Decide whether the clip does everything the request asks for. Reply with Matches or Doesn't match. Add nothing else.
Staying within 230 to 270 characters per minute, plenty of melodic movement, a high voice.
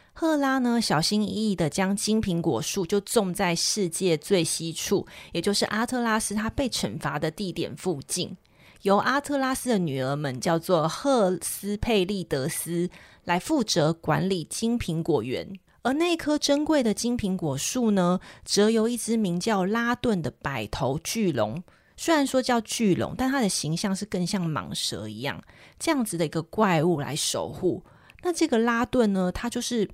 Matches